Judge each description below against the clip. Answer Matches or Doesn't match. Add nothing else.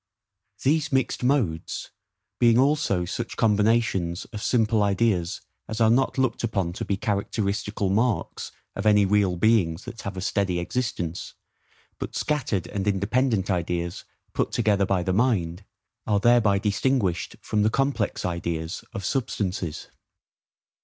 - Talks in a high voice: Doesn't match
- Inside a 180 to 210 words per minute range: Doesn't match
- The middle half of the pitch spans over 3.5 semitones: Matches